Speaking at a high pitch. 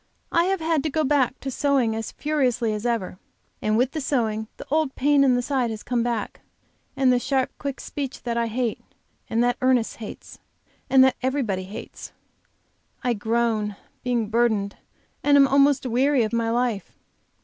Yes: high, 245 Hz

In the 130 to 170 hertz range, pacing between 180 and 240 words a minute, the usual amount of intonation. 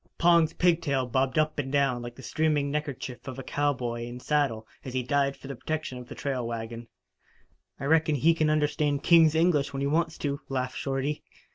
Yes: medium, 140 Hz; average, 195 wpm; average, 3.2 semitones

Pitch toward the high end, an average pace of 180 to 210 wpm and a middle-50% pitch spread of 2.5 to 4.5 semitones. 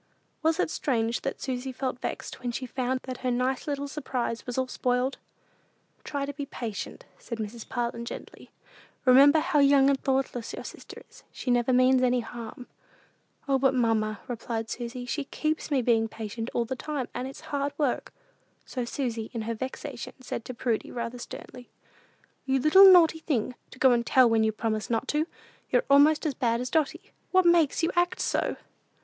Yes: very high, 255 Hz; average, 190 wpm; average, 3.0 semitones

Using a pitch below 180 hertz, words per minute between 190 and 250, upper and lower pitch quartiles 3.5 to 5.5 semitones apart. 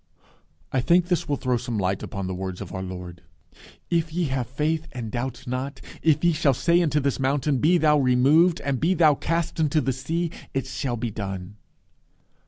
Yes: low, 135 Hz; average, 195 wpm; average, 4.9 semitones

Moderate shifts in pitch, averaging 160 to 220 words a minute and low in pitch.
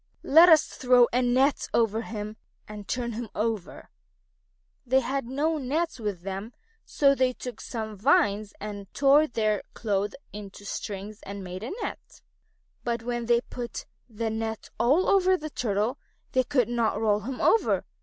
No: average, 3.7 semitones; average, 165 wpm; high, 235 Hz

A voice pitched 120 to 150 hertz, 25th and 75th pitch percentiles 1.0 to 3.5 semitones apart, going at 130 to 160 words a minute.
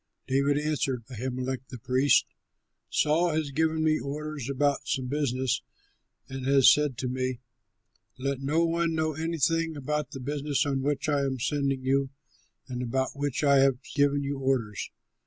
Yes: medium, 140 Hz; narrow, 2.4 semitones; average, 155 wpm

